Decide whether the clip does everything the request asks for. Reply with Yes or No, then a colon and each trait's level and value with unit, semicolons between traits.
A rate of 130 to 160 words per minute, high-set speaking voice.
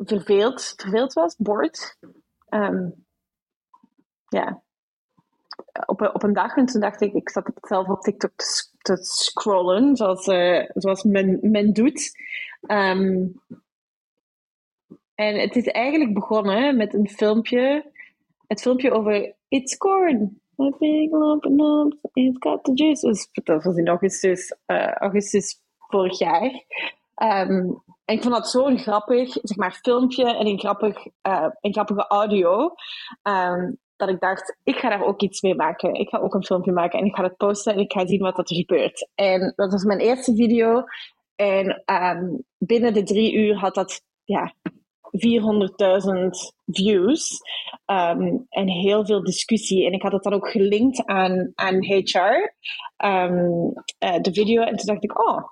Yes: average, 155 wpm; high, 210 Hz